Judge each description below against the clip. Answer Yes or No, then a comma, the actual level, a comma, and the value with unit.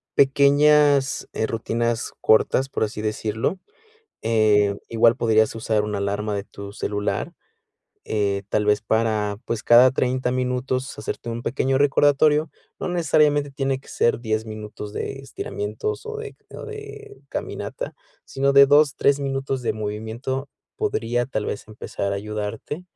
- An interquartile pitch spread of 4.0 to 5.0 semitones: Yes, average, 4.5 semitones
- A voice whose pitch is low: Yes, low, 120 Hz